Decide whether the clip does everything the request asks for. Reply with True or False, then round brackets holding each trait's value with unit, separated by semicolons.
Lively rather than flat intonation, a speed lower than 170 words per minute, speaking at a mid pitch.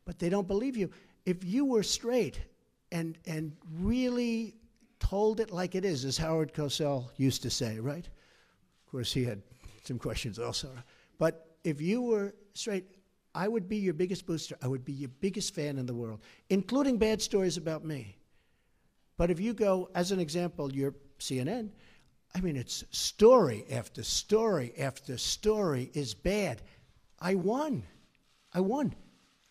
True (6.8 semitones; 160 wpm; 175 Hz)